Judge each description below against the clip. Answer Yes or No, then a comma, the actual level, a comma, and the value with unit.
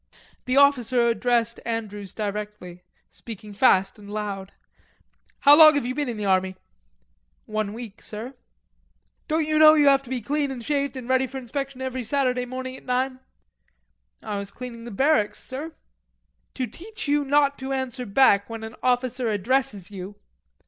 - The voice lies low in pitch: No, very high, 250 Hz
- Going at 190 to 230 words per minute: No, average, 165 wpm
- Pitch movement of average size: Yes, average, 4.4 semitones